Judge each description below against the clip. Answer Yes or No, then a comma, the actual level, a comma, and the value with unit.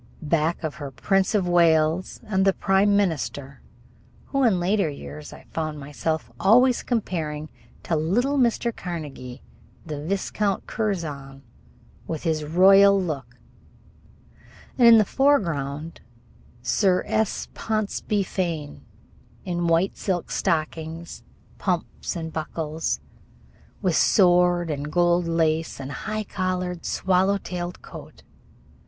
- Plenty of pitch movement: No, average, 4.0 semitones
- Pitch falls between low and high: Yes, medium, 175 Hz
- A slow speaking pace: Yes, slow, 120 wpm